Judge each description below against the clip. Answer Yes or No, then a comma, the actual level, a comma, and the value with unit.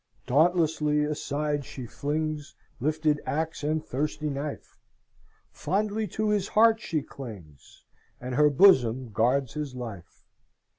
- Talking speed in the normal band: No, slow, 115 wpm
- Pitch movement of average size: Yes, average, 3.3 semitones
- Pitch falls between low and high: Yes, medium, 150 Hz